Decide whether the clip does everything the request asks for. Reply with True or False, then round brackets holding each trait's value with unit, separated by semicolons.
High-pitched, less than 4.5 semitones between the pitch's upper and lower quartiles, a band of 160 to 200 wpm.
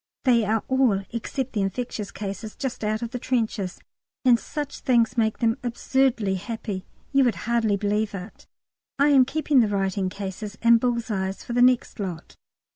True (225 Hz; 3.5 semitones; 175 wpm)